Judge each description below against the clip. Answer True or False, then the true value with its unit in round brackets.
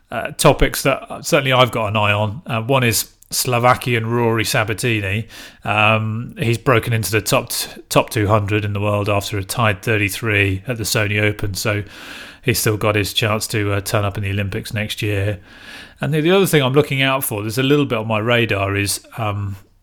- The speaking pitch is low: True (110 Hz)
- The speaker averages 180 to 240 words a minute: True (205 wpm)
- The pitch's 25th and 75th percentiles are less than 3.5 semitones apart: True (2.7 semitones)